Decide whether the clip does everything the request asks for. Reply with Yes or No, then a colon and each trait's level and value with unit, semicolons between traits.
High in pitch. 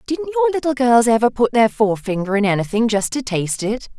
Yes: high, 240 Hz